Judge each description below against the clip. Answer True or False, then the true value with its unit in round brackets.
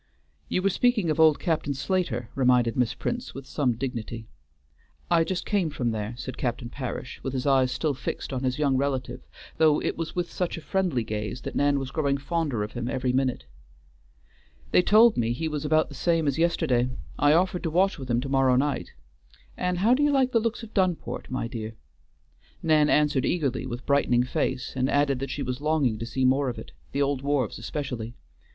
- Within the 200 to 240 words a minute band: True (205 wpm)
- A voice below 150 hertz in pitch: True (140 Hz)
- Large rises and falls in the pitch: False (4.4 semitones)